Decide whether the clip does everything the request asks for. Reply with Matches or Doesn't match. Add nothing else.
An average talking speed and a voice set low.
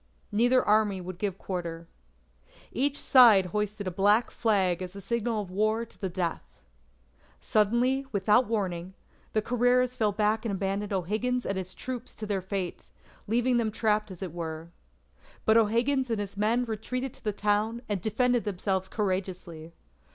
Doesn't match